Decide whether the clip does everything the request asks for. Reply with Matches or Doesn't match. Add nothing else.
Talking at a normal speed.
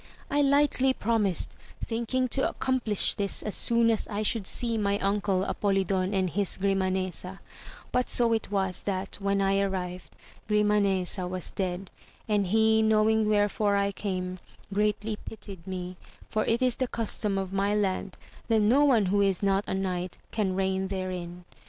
Matches